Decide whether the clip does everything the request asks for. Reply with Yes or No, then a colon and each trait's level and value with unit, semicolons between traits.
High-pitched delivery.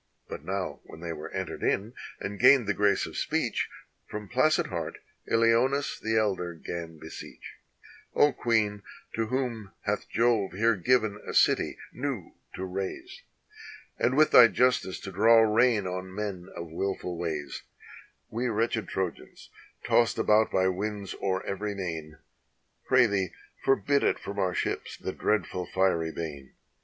No: low, 105 Hz